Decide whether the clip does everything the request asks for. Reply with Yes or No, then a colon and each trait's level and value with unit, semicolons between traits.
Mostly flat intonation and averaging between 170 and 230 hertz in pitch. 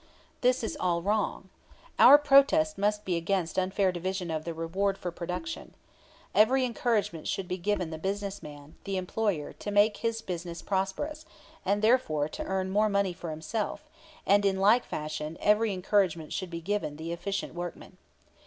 No: average, 3.6 semitones; high, 190 Hz